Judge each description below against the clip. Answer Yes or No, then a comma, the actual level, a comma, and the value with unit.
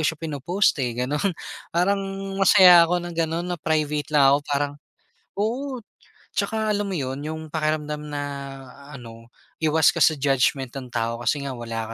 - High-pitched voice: No, medium, 150 Hz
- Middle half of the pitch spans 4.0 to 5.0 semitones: Yes, average, 4.3 semitones